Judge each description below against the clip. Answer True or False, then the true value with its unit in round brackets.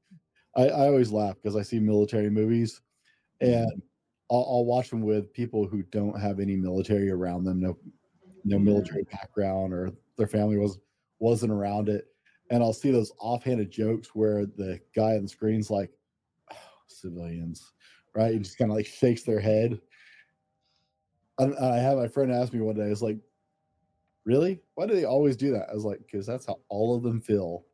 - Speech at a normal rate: True (195 wpm)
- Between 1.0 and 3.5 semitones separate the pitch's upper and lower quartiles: True (3.1 semitones)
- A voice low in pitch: True (110 Hz)